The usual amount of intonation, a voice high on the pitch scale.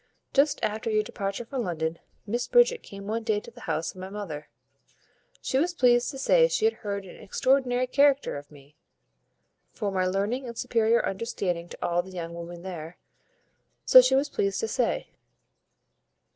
No: wide, 5.9 semitones; high, 215 Hz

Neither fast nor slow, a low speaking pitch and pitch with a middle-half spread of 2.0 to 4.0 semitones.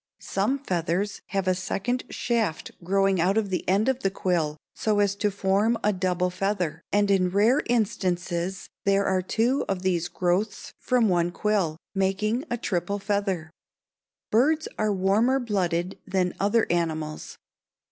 No: average, 150 wpm; high, 195 Hz; average, 2.8 semitones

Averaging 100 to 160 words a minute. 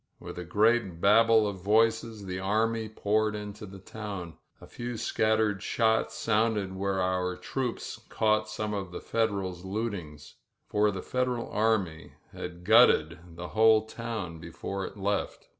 Yes: average, 150 wpm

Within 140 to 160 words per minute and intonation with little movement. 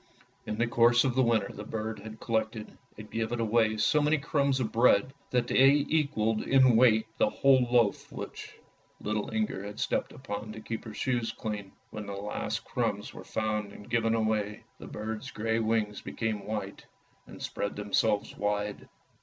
No: average, 180 wpm; narrow, 2.3 semitones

